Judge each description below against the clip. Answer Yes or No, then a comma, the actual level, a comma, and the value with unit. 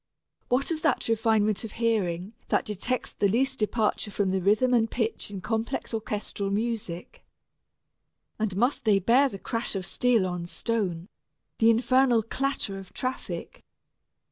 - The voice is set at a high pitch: Yes, high, 220 Hz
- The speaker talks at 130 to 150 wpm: Yes, average, 145 wpm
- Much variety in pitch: No, average, 3.6 semitones